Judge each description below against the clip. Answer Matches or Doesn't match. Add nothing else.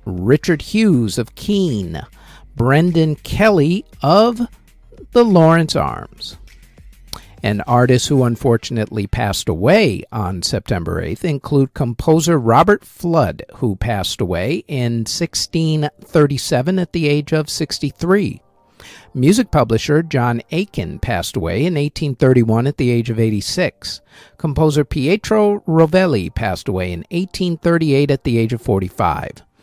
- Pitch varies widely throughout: Matches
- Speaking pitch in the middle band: Matches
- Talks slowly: Matches